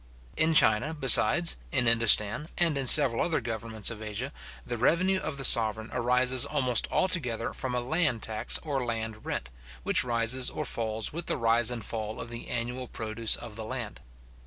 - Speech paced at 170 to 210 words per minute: Yes, average, 180 wpm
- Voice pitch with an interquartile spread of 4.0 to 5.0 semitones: No, average, 3.3 semitones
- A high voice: No, low, 120 Hz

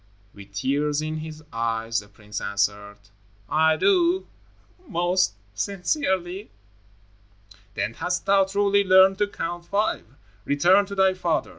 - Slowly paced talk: Yes, slow, 125 wpm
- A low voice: No, medium, 175 Hz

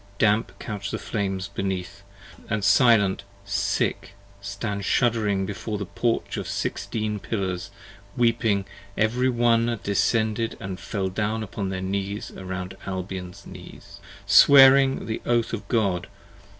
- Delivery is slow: Yes, slow, 125 wpm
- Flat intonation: No, average, 3.0 semitones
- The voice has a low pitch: Yes, low, 105 Hz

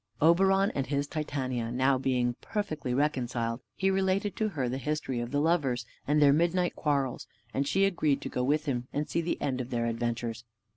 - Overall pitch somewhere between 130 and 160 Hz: Yes, medium, 140 Hz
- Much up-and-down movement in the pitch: No, average, 4.9 semitones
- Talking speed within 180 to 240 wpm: Yes, average, 195 wpm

